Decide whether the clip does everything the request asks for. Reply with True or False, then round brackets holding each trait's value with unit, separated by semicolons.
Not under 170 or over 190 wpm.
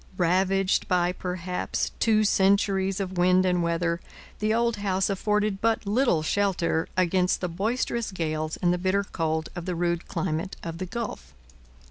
False (155 wpm)